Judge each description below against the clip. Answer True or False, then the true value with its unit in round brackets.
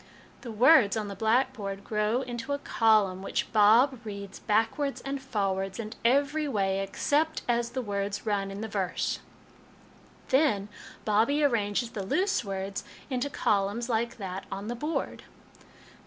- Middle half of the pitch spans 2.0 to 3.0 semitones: False (4.5 semitones)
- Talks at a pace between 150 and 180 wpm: True (155 wpm)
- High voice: True (220 Hz)